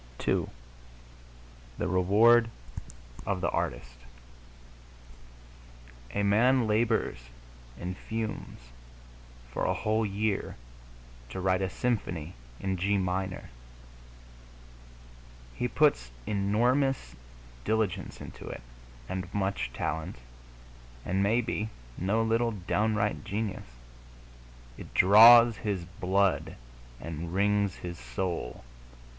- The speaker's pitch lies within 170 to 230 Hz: No, low, 100 Hz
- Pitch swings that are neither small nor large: Yes, average, 3.4 semitones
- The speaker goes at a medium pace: No, slow, 95 wpm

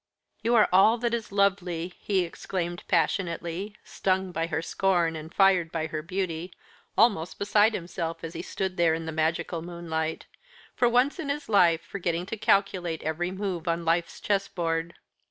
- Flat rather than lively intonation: No, average, 3.1 semitones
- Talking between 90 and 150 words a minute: No, average, 165 wpm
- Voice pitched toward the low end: No, medium, 175 Hz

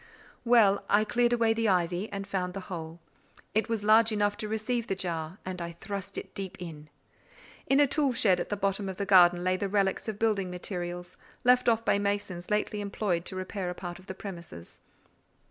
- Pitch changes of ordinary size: Yes, average, 3.0 semitones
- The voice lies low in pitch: No, high, 195 Hz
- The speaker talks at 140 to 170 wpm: No, average, 200 wpm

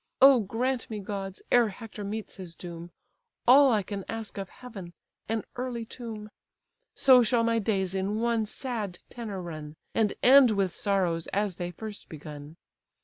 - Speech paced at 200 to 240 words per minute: No, average, 160 wpm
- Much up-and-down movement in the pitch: No, average, 3.6 semitones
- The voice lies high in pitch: Yes, high, 210 Hz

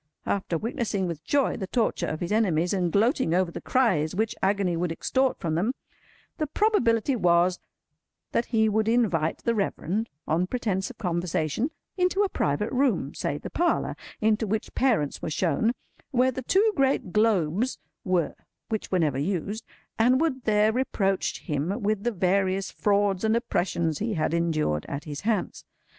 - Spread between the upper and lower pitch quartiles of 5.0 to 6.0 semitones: Yes, average, 5.3 semitones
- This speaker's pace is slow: No, average, 160 wpm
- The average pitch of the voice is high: Yes, high, 200 Hz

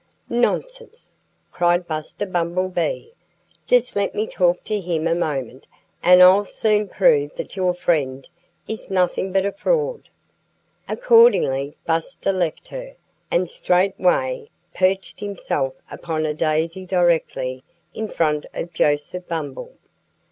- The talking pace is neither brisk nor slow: No, slow, 120 wpm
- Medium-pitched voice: Yes, medium, 180 Hz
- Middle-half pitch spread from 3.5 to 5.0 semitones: Yes, average, 4.6 semitones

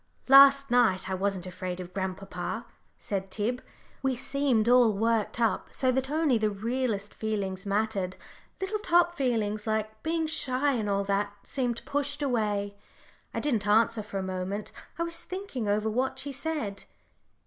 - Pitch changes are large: No, average, 5.0 semitones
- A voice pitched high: Yes, high, 220 Hz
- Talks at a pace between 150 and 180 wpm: Yes, average, 160 wpm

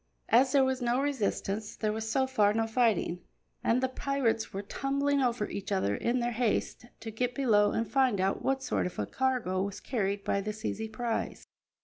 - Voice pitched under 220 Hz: No, high, 230 Hz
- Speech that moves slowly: No, average, 200 wpm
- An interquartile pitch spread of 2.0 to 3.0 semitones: No, average, 4.0 semitones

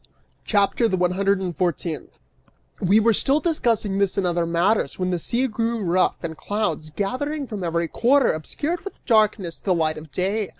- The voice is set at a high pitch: Yes, high, 195 Hz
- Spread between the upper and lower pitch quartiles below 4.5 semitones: No, average, 4.8 semitones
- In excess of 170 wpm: Yes, average, 180 wpm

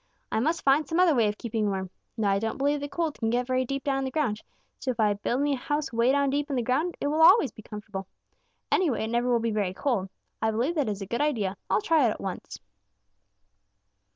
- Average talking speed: No, fast, 255 wpm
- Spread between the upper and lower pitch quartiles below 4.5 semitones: No, average, 5.1 semitones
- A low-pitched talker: No, high, 245 Hz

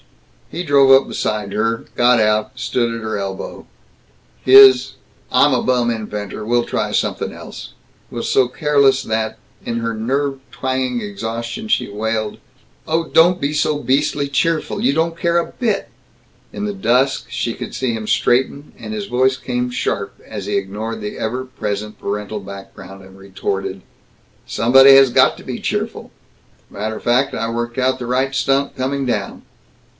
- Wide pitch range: No, average, 4.0 semitones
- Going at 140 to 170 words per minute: Yes, average, 160 wpm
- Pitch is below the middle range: Yes, low, 125 Hz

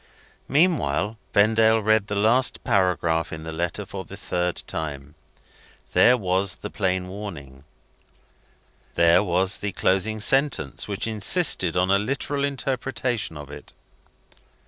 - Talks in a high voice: No, low, 100 Hz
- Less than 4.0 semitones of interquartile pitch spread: No, average, 4.3 semitones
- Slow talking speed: Yes, slow, 125 wpm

